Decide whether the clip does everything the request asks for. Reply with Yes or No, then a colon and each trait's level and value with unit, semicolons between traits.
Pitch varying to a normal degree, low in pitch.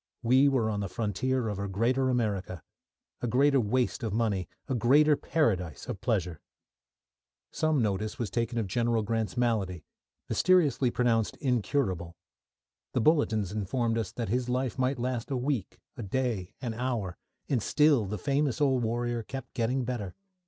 Yes: average, 3.6 semitones; low, 120 Hz